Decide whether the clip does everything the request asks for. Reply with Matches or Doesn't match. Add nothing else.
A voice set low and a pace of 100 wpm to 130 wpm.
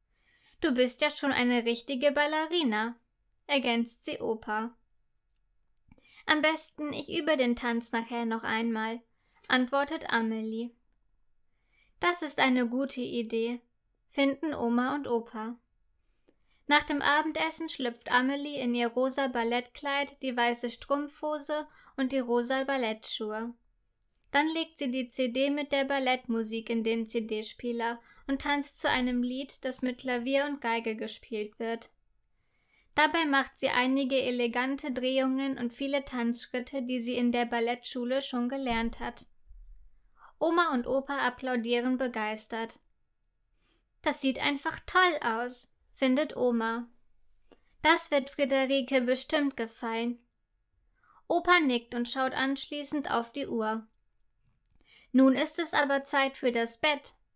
Doesn't match